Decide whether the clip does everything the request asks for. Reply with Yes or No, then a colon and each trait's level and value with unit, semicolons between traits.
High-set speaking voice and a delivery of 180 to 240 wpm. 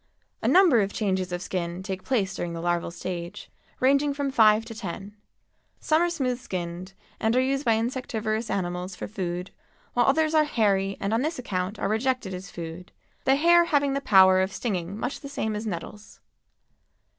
Yes: high, 215 Hz; average, 185 wpm